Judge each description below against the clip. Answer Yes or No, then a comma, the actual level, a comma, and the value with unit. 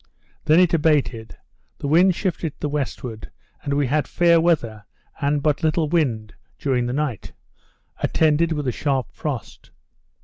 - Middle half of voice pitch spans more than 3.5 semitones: Yes, average, 4.0 semitones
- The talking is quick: No, average, 150 wpm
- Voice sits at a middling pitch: Yes, medium, 150 Hz